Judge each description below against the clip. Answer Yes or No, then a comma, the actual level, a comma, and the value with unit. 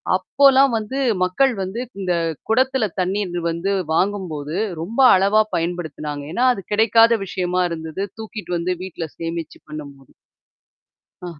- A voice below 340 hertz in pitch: Yes, medium, 185 Hz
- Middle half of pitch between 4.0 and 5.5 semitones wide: Yes, average, 4.7 semitones